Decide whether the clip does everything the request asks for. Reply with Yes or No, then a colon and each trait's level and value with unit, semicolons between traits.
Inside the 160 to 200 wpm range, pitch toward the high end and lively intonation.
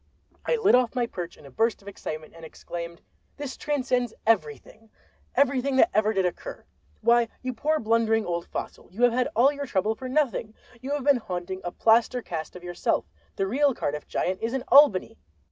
Yes: average, 185 wpm; high, 225 Hz; wide, 6.2 semitones